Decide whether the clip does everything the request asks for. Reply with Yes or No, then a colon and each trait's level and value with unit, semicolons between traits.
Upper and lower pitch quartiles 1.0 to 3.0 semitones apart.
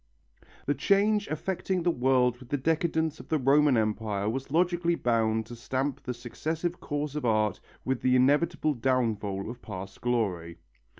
No: wide, 5.6 semitones